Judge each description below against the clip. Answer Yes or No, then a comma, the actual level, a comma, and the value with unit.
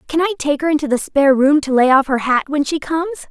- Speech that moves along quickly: Yes, fast, 290 wpm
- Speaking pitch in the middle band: No, very high, 290 Hz